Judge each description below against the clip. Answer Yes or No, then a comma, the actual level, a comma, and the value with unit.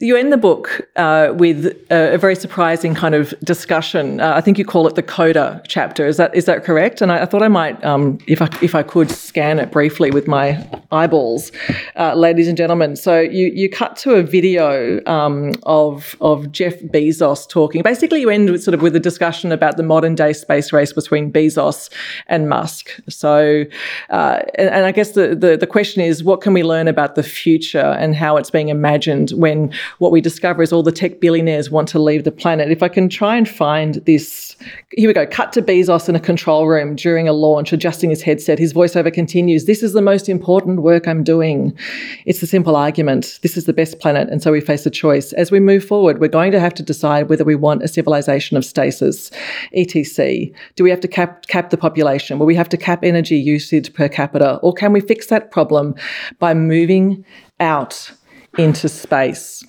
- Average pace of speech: No, fast, 215 wpm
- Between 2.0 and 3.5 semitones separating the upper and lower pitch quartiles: Yes, average, 2.9 semitones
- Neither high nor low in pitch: Yes, medium, 165 Hz